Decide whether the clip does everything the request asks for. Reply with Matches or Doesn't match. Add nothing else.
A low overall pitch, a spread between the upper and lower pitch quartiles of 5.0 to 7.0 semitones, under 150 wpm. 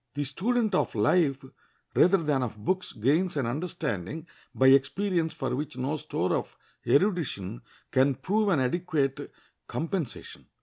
Doesn't match